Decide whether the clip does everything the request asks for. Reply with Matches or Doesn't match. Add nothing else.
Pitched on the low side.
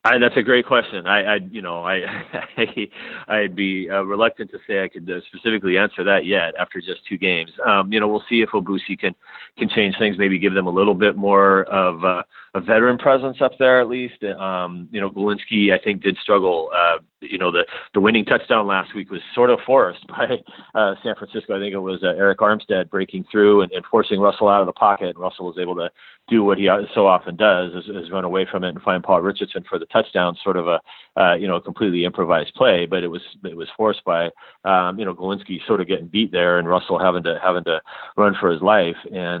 Matches